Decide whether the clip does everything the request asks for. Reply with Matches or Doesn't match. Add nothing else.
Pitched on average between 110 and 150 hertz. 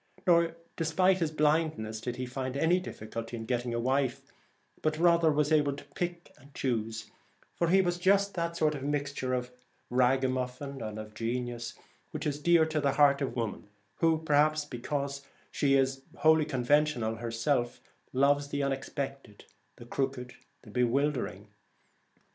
Matches